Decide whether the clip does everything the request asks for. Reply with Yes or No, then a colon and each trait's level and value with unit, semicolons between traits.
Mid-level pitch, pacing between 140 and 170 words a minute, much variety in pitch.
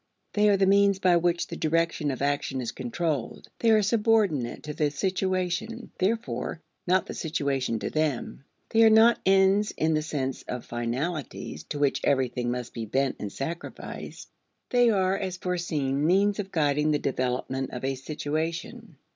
Yes: medium, 160 Hz; average, 165 wpm; wide, 6.2 semitones